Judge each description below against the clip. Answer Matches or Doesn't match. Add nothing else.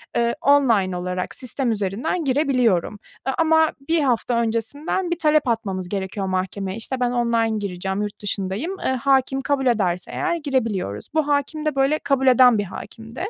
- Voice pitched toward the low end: Doesn't match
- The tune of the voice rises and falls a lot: Matches